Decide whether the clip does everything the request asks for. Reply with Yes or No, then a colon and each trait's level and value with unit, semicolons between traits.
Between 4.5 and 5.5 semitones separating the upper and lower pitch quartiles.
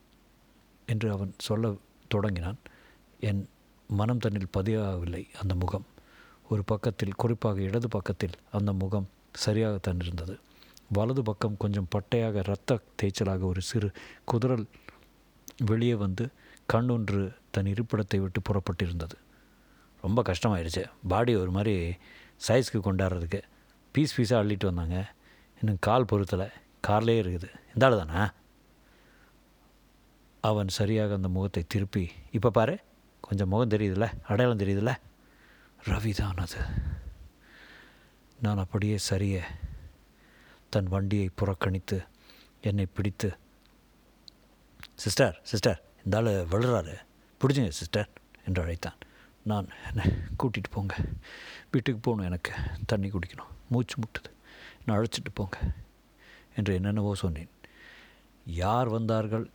No: average, 2.8 semitones